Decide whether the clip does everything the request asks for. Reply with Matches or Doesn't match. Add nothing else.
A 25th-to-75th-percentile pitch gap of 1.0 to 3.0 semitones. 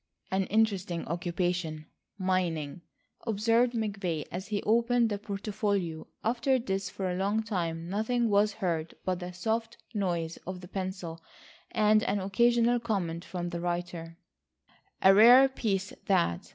Doesn't match